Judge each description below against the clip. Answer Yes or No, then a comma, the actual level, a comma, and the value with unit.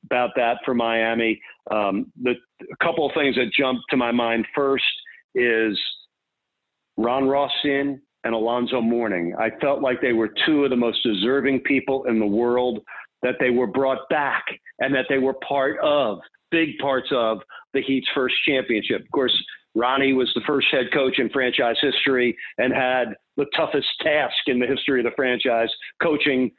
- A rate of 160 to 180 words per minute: Yes, average, 175 wpm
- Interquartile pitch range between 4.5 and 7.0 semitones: No, average, 2.7 semitones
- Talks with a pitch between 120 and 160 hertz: Yes, low, 125 Hz